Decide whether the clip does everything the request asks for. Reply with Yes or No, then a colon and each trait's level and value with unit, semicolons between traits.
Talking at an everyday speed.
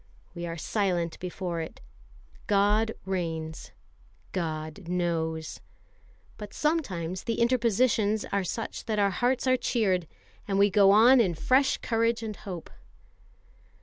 No: slow, 125 wpm